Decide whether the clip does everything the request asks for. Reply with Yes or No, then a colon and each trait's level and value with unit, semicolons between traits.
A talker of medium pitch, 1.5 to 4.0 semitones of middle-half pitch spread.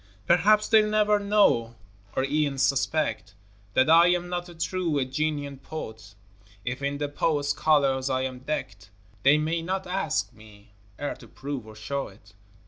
No: medium, 145 Hz; average, 4.8 semitones